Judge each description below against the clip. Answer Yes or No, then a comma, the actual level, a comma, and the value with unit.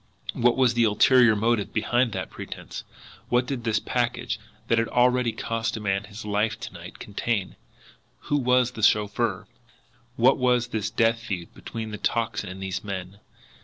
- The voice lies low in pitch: Yes, low, 115 Hz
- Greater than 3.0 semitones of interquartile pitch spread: No, average, 2.7 semitones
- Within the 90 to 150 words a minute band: No, average, 165 wpm